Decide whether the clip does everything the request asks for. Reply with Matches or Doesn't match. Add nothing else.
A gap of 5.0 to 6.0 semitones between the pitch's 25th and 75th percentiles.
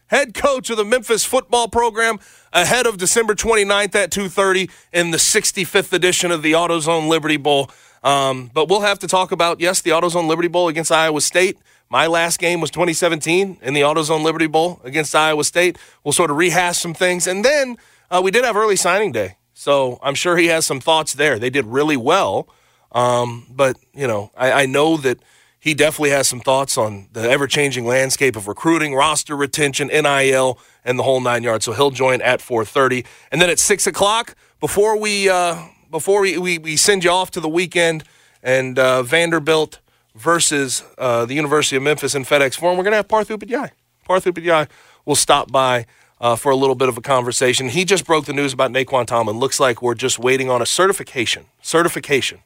Matches